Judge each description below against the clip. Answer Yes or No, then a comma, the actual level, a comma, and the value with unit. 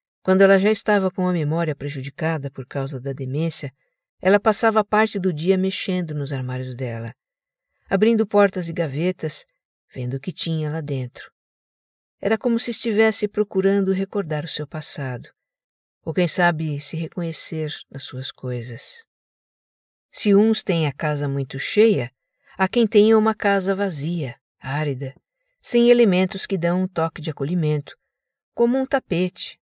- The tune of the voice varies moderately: No, wide, 6.2 semitones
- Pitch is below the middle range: No, medium, 175 Hz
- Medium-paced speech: Yes, average, 150 wpm